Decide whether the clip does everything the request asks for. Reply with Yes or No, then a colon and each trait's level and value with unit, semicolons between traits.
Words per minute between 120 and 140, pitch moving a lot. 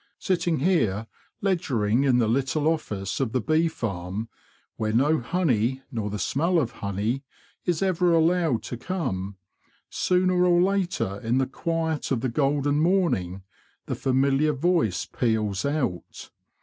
Yes: slow, 135 wpm; wide, 7.1 semitones